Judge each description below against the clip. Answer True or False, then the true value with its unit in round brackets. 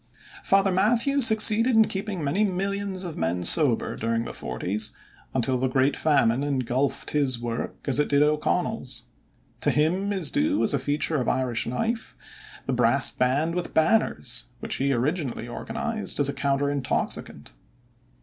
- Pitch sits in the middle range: True (145 Hz)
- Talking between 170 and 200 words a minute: False (155 wpm)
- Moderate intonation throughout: False (7.4 semitones)